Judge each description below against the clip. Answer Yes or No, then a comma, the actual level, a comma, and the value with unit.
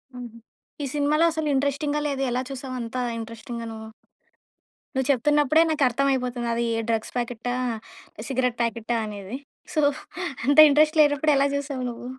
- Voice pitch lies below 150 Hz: No, very high, 260 Hz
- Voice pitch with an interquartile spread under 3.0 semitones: No, average, 3.5 semitones